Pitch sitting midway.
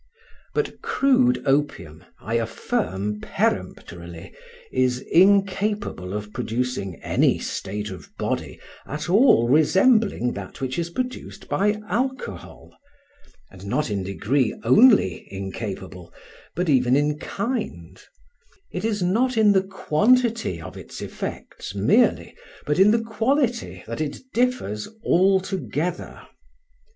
Yes: medium, 155 Hz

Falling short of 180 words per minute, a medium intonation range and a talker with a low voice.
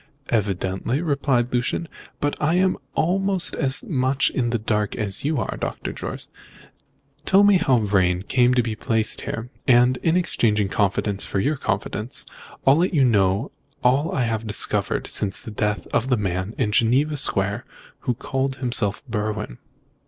Yes: average, 155 wpm; average, 4.7 semitones; low, 120 Hz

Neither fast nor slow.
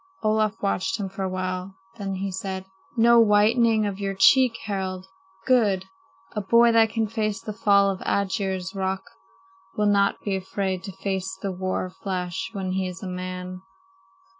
Yes: average, 165 wpm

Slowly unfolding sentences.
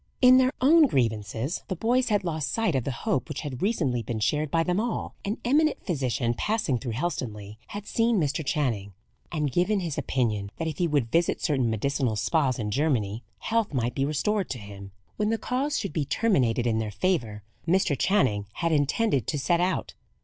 No: average, 195 wpm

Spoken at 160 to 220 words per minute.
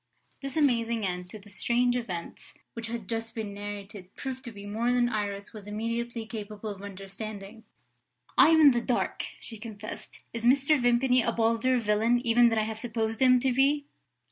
Yes: average, 185 wpm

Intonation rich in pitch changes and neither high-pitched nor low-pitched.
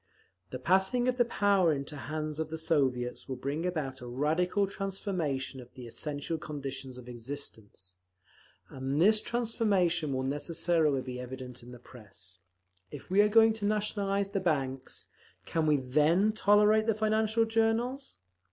Yes: wide, 7.5 semitones; medium, 160 Hz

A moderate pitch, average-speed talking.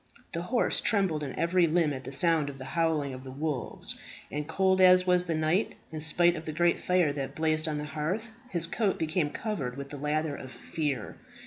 No: medium, 155 Hz; fast, 215 wpm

